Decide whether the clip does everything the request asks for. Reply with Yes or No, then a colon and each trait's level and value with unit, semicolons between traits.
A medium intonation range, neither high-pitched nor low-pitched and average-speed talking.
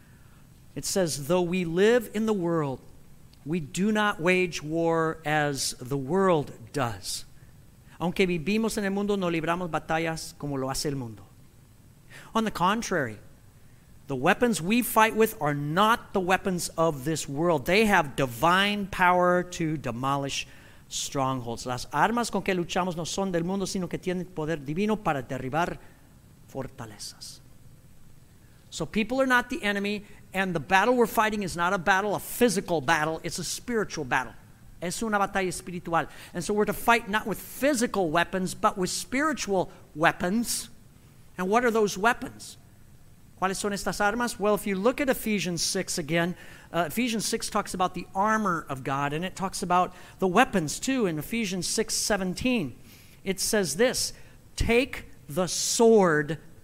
No: wide, 6.5 semitones; medium, 175 Hz; average, 160 wpm